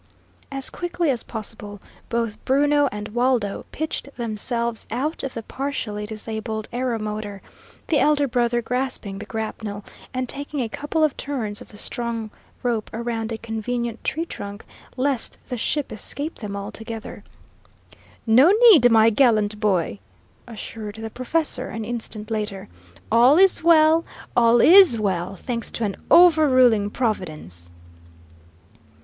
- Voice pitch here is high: Yes, high, 230 Hz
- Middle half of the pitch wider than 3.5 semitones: Yes, average, 4.0 semitones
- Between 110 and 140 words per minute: Yes, slow, 135 wpm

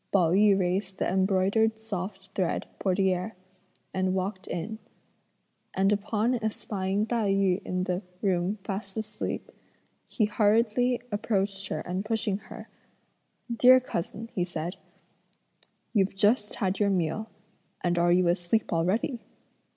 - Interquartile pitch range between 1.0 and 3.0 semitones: Yes, average, 2.7 semitones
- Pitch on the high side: Yes, high, 195 Hz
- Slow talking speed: Yes, slow, 130 wpm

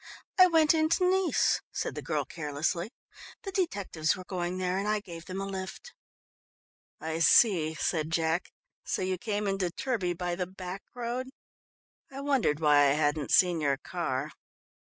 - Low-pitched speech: No, medium, 185 Hz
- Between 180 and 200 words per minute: No, average, 160 wpm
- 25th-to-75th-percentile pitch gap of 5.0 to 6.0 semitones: Yes, wide, 5.4 semitones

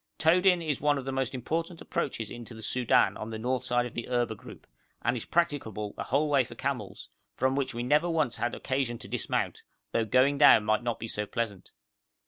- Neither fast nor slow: No, fast, 215 wpm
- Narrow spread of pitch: No, average, 3.7 semitones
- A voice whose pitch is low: Yes, low, 125 Hz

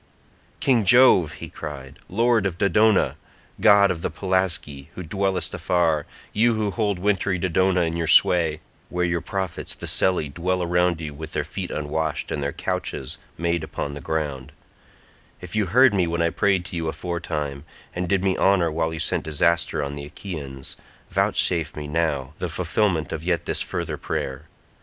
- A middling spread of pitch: Yes, average, 3.6 semitones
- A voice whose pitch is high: No, very low, 85 Hz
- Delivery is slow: No, average, 170 wpm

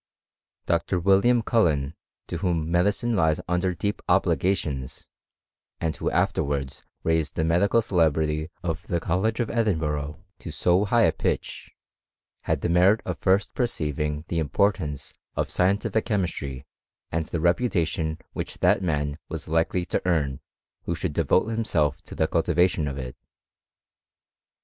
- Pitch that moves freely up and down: No, average, 4.0 semitones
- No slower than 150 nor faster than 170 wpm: No, average, 140 wpm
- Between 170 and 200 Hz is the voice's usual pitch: No, very low, 85 Hz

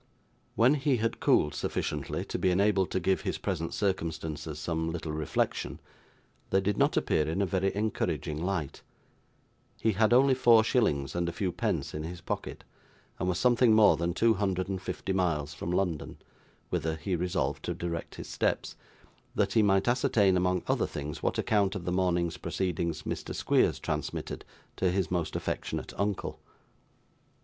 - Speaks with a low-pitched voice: Yes, very low, 90 Hz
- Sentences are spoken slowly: No, average, 170 wpm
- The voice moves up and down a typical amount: Yes, average, 3.7 semitones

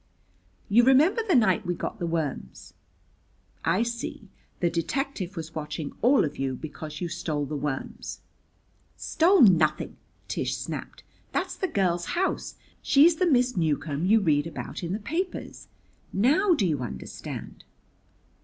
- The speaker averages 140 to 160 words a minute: Yes, average, 145 wpm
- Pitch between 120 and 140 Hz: No, medium, 185 Hz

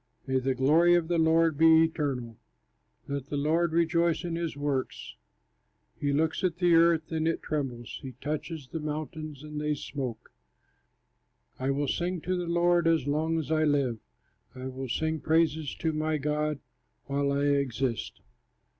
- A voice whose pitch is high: No, medium, 155 Hz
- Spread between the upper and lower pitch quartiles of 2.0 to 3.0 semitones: Yes, average, 2.7 semitones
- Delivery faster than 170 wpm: No, average, 165 wpm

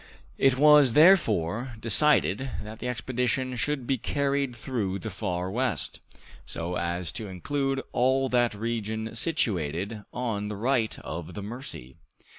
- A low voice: Yes, low, 115 Hz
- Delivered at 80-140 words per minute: Yes, slow, 135 wpm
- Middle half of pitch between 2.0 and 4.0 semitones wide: No, average, 4.7 semitones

